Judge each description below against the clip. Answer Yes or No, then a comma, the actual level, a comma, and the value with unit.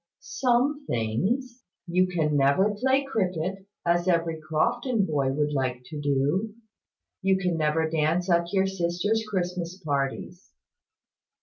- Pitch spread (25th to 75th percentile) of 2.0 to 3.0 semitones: No, average, 4.4 semitones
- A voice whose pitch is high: No, medium, 175 Hz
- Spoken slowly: Yes, slow, 125 wpm